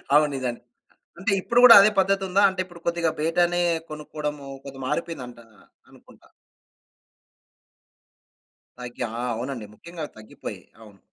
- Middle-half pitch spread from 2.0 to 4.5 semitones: No, average, 5.3 semitones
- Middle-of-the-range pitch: Yes, medium, 155 Hz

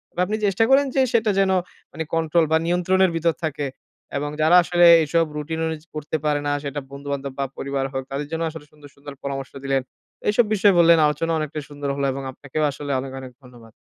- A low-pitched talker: No, medium, 150 Hz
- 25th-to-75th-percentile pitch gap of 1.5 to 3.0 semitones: No, average, 3.4 semitones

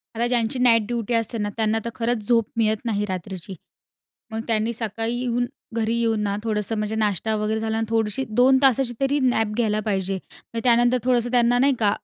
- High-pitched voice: Yes, high, 225 Hz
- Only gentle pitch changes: Yes, narrow, 2.2 semitones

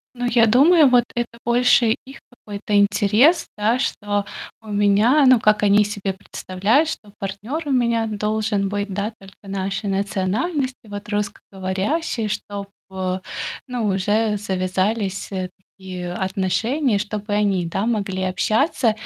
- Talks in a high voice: Yes, high, 210 Hz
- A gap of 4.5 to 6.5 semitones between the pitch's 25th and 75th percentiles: No, average, 3.0 semitones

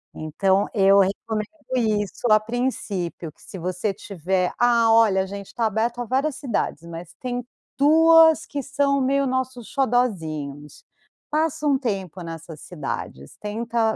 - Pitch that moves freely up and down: Yes, wide, 5.8 semitones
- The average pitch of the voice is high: Yes, high, 220 Hz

